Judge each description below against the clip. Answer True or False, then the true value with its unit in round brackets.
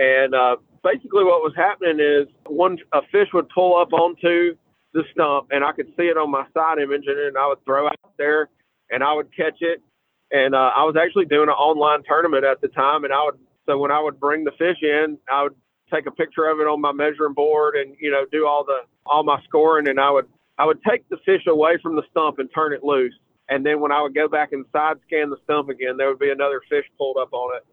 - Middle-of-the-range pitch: True (150 Hz)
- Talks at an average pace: False (255 wpm)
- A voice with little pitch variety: True (2.2 semitones)